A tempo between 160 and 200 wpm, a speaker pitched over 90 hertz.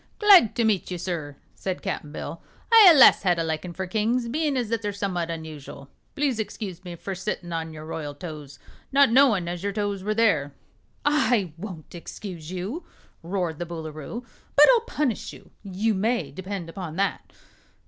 Yes: average, 180 wpm; high, 190 Hz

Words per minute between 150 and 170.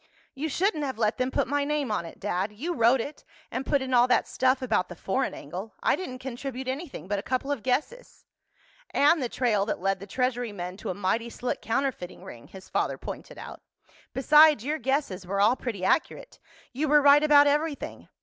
No: fast, 205 wpm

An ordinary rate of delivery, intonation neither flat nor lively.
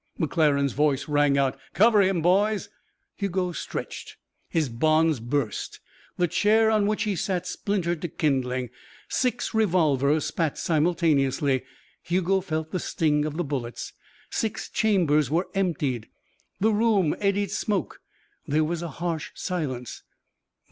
No: slow, 130 wpm; average, 5.0 semitones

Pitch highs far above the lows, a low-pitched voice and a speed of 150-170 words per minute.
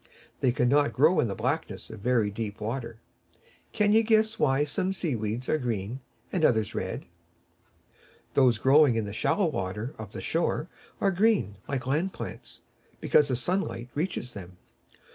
Yes: wide, 6.6 semitones; low, 130 Hz; average, 160 wpm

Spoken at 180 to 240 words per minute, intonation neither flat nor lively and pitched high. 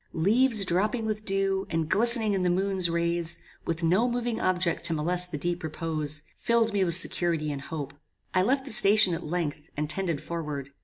No: average, 190 wpm; average, 3.9 semitones; medium, 175 Hz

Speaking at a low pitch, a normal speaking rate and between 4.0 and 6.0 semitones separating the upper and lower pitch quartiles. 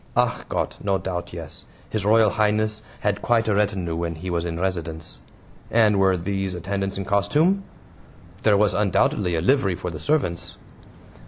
No: very low, 95 Hz; average, 165 wpm; average, 3.4 semitones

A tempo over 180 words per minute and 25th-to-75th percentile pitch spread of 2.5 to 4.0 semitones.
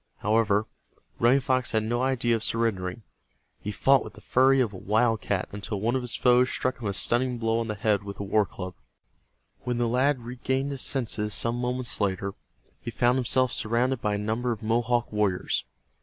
Yes: average, 195 wpm; average, 2.9 semitones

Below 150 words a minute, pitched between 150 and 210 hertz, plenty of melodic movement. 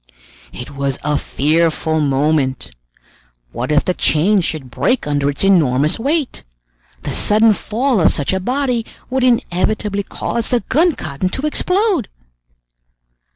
Yes: slow, 135 wpm; medium, 185 Hz; wide, 9.0 semitones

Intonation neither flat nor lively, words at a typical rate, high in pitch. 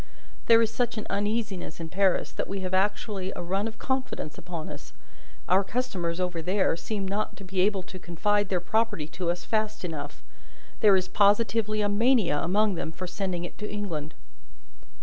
Yes: average, 3.2 semitones; average, 190 wpm; high, 195 Hz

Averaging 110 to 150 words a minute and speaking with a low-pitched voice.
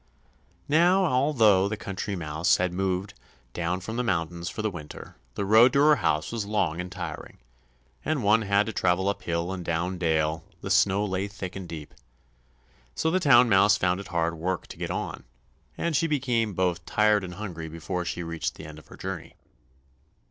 No: average, 190 wpm; very low, 95 Hz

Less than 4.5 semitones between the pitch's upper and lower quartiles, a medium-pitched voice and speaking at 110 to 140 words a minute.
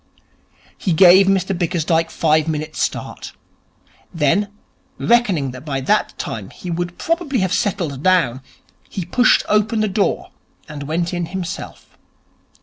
Yes: average, 4.1 semitones; medium, 175 Hz; slow, 135 wpm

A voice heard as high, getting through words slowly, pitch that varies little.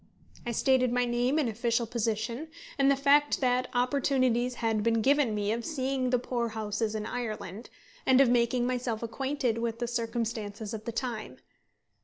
No: high, 240 Hz; average, 170 wpm; narrow, 2.2 semitones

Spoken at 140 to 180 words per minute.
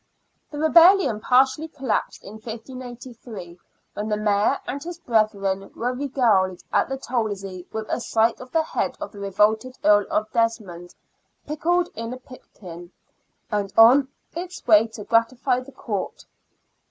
Yes: average, 150 wpm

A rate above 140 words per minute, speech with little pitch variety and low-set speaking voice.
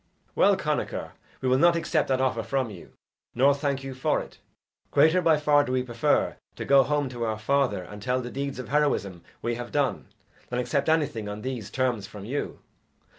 No: average, 200 wpm; average, 3.3 semitones; low, 130 Hz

